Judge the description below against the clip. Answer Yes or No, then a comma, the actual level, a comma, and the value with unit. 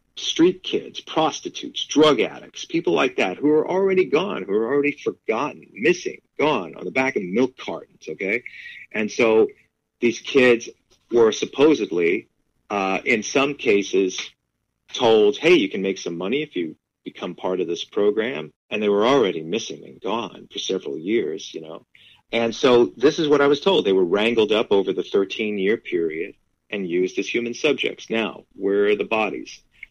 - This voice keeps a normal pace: Yes, average, 175 wpm